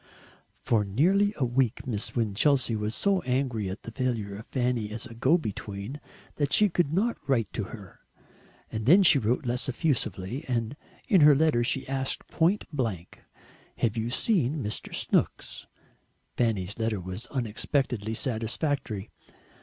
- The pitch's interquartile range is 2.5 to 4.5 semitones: No, average, 4.9 semitones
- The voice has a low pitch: Yes, low, 120 Hz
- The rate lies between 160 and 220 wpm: No, average, 150 wpm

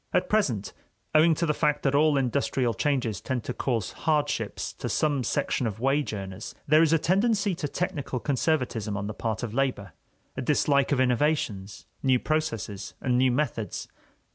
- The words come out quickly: No, average, 170 wpm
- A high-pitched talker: No, low, 135 Hz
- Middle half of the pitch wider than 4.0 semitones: Yes, average, 5.0 semitones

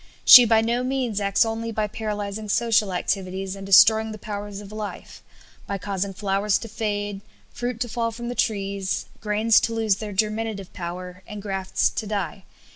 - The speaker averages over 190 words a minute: No, average, 175 wpm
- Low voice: No, high, 210 Hz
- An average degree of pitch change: No, narrow, 2.2 semitones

